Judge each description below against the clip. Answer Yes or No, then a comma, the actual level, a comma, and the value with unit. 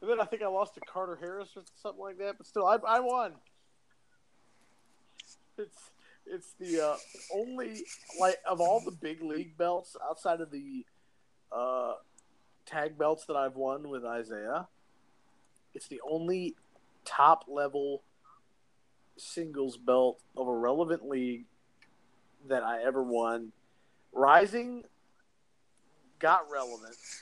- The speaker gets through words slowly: Yes, slow, 130 wpm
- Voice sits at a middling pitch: Yes, medium, 165 Hz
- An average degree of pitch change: No, wide, 6.9 semitones